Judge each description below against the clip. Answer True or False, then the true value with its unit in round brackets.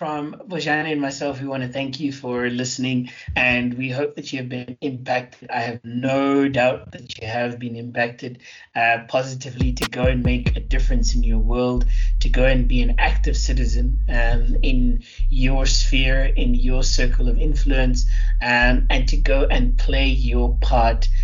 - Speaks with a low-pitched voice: True (125 Hz)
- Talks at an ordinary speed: True (180 wpm)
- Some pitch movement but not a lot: False (1.7 semitones)